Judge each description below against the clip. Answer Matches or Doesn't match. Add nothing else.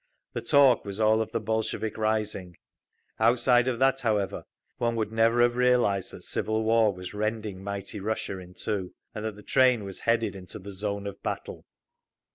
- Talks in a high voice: Doesn't match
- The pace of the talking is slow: Doesn't match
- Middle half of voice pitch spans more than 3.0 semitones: Doesn't match